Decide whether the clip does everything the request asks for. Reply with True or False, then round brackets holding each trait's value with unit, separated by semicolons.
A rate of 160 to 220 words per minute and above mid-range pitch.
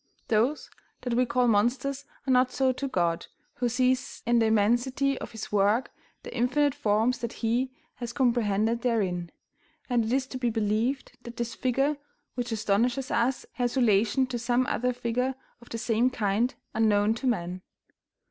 True (165 wpm; 240 Hz)